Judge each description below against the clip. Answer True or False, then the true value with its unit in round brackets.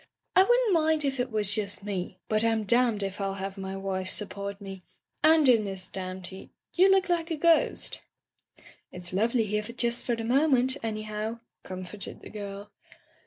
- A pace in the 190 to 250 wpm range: True (195 wpm)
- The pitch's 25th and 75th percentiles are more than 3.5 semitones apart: True (4.7 semitones)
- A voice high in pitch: True (215 Hz)